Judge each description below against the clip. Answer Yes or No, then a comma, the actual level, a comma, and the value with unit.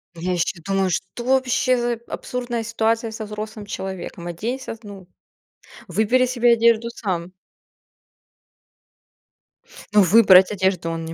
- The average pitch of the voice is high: Yes, high, 210 Hz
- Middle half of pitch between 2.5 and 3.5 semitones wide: No, average, 4.1 semitones